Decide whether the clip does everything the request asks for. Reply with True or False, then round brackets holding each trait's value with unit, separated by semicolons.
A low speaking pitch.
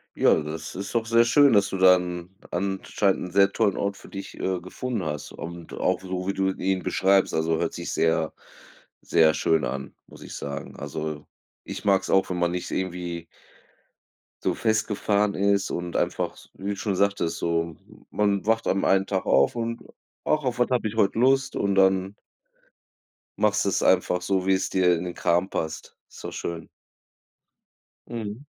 True (95 Hz)